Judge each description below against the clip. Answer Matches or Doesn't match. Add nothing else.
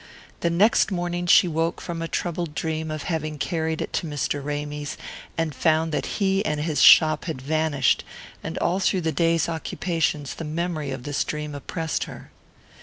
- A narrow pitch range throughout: Matches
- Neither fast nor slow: Matches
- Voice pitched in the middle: Matches